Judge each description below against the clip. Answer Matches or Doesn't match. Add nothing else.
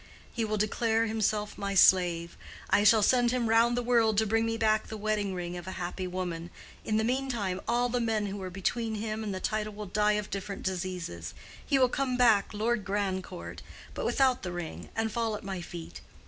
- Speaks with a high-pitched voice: Matches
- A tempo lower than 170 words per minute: Doesn't match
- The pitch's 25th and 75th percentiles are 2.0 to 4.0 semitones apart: Matches